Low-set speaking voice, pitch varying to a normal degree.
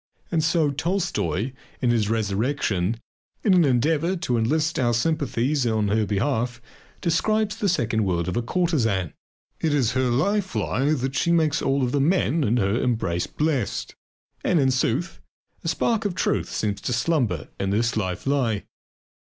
No: low, 130 Hz; wide, 6.4 semitones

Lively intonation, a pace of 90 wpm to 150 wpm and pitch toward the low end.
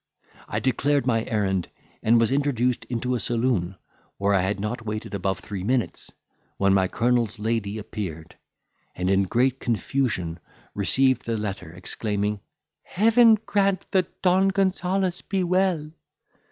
Yes: wide, 6.3 semitones; average, 140 wpm; low, 115 Hz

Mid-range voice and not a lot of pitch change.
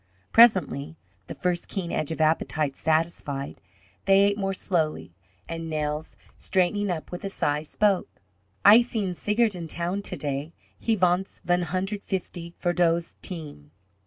No: medium, 175 Hz; average, 3.6 semitones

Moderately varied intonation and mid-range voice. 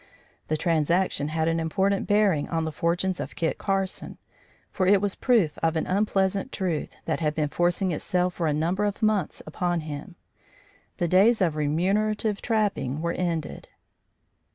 Yes: average, 3.6 semitones; medium, 175 Hz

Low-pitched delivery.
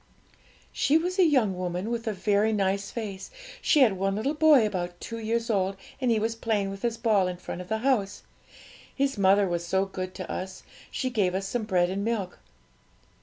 No: high, 205 Hz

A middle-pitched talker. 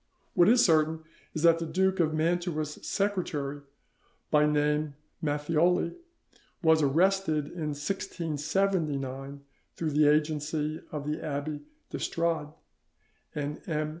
Yes: medium, 155 Hz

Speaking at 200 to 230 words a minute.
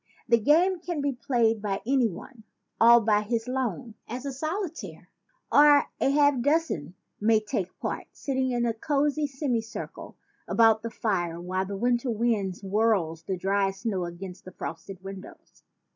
No: average, 170 wpm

